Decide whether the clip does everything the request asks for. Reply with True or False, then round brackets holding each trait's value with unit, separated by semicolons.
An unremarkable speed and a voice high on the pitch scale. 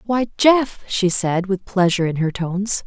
True (190 wpm; 195 Hz)